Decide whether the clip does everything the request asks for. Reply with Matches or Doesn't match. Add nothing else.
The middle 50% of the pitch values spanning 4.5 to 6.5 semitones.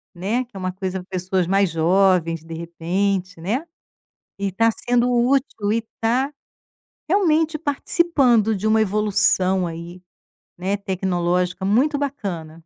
Matches